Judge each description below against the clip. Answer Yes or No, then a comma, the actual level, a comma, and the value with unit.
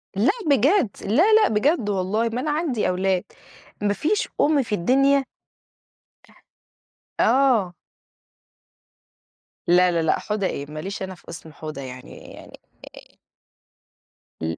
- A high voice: Yes, high, 210 Hz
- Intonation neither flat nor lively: No, wide, 7.4 semitones